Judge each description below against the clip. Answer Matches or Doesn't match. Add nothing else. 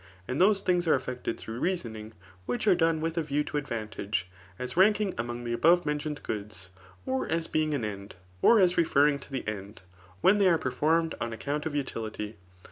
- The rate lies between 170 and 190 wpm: Doesn't match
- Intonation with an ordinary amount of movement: Doesn't match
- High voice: Doesn't match